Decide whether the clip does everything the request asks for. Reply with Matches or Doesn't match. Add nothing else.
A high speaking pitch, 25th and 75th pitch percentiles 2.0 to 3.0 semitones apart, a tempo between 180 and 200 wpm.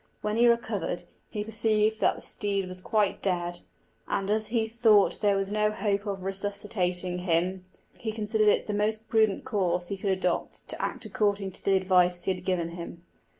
Matches